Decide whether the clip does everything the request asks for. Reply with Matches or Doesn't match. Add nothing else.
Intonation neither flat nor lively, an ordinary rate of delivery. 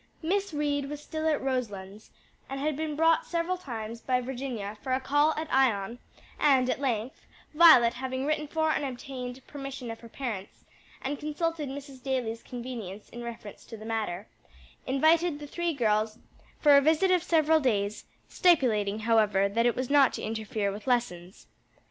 Matches